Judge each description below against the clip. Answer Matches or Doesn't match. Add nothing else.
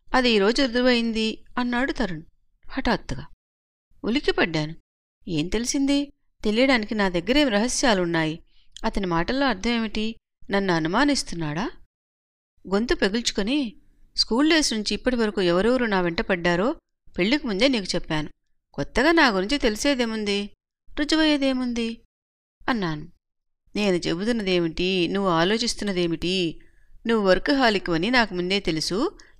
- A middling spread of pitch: Doesn't match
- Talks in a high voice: Matches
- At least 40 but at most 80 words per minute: Doesn't match